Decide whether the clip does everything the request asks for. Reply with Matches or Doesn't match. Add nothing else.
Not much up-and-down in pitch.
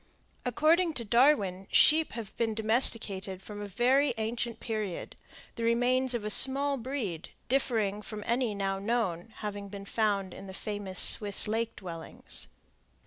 Doesn't match